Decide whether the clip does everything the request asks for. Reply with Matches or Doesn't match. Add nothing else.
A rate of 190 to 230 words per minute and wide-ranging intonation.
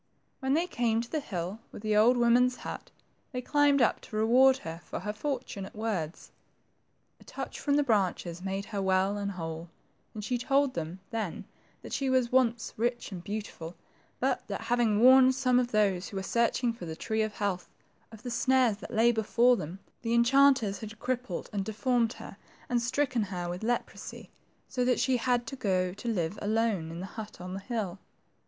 Doesn't match